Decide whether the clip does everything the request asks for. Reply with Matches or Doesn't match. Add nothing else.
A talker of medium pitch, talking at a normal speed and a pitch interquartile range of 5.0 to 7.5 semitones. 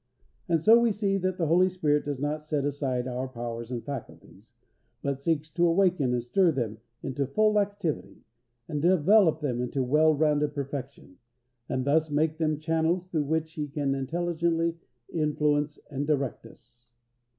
Doesn't match